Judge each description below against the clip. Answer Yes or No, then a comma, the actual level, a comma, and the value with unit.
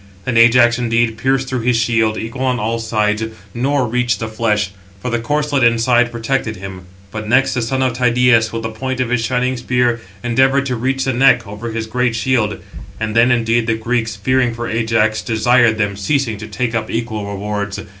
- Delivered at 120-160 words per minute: No, average, 195 wpm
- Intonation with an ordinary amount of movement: No, narrow, 2.0 semitones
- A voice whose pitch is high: No, low, 115 Hz